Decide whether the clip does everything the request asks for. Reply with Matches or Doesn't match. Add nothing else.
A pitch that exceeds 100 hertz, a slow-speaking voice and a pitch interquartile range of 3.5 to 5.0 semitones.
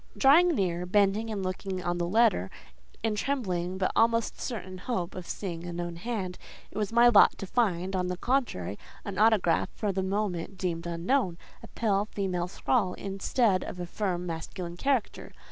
Doesn't match